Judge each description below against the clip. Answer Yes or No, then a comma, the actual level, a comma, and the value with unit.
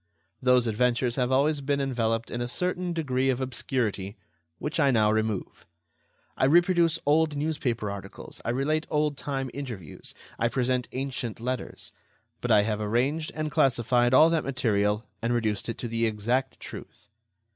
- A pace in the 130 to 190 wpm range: Yes, average, 155 wpm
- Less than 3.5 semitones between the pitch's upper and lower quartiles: No, average, 3.8 semitones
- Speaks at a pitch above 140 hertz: No, low, 125 Hz